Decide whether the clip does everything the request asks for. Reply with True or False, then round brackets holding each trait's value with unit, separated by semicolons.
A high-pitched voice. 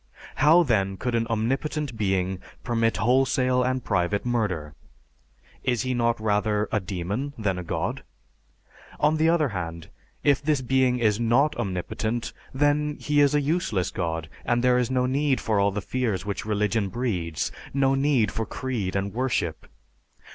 False (115 Hz)